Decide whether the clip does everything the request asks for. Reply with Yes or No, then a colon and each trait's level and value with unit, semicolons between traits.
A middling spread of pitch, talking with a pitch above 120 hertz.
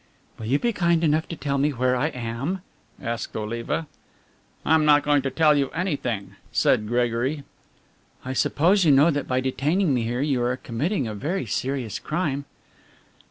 Yes: average, 4.2 semitones; medium, 140 Hz